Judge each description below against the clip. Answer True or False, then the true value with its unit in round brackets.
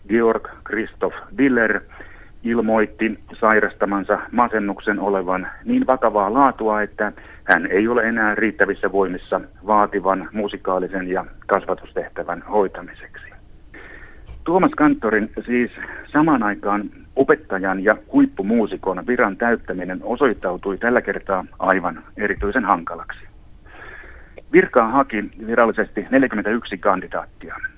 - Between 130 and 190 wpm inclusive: False (95 wpm)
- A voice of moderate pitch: False (110 Hz)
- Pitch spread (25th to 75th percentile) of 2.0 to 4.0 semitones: True (2.9 semitones)